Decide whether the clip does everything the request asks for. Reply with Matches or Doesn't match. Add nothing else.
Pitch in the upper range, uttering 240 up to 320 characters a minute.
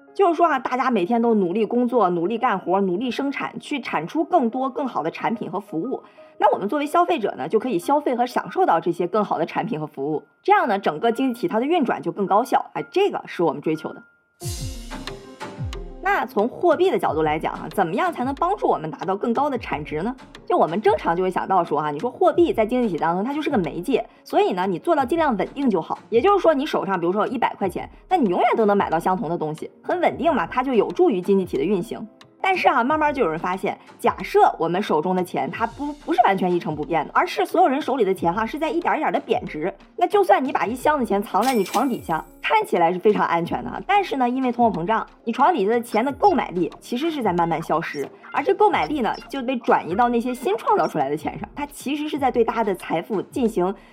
Doesn't match